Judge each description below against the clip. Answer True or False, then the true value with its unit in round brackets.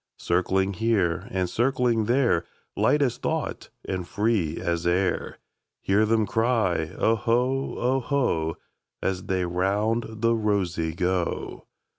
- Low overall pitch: True (100 Hz)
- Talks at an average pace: False (100 wpm)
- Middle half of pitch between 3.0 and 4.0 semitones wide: False (4.5 semitones)